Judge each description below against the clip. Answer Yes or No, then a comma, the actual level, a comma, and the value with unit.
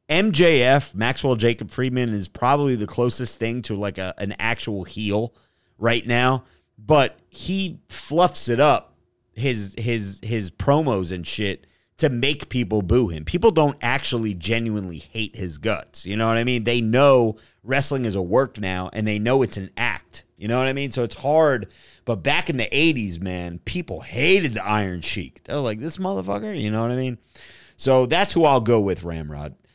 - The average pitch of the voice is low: Yes, low, 115 Hz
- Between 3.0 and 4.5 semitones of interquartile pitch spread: No, average, 4.9 semitones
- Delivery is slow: No, average, 190 wpm